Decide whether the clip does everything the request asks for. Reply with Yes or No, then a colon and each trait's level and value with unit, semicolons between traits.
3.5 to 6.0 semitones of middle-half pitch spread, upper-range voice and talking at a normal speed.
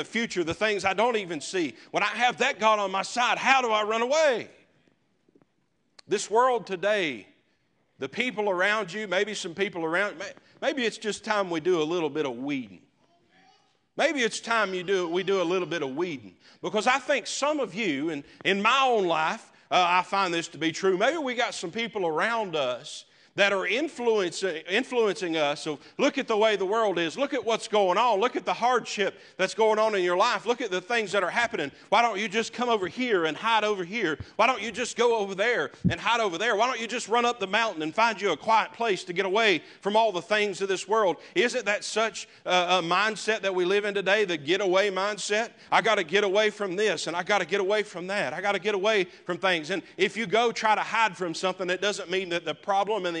No: average, 3.8 semitones; high, 210 Hz; fast, 240 wpm